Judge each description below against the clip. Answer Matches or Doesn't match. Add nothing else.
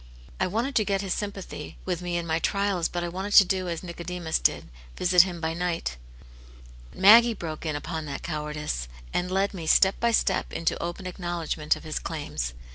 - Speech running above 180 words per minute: Matches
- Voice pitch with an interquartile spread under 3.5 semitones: Matches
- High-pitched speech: Doesn't match